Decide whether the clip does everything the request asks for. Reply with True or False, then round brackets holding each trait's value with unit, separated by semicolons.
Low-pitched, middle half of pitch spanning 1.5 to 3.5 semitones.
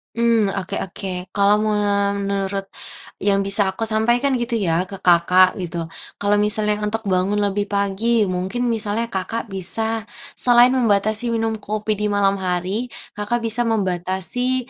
False (205 Hz; 2.6 semitones)